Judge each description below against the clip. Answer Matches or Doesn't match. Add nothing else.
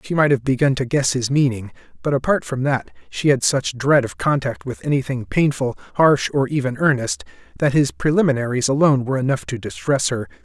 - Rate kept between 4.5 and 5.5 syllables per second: Doesn't match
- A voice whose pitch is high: Doesn't match